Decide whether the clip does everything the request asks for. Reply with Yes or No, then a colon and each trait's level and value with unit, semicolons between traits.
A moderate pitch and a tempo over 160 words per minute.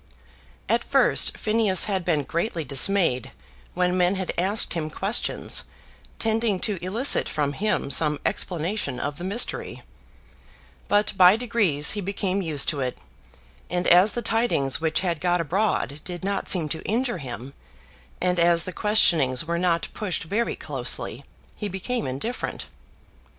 No: medium, 180 Hz; average, 145 wpm